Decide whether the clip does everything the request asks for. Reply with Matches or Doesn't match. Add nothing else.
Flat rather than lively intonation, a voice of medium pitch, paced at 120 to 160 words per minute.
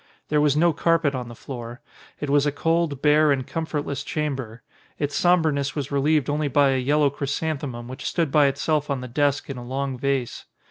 Doesn't match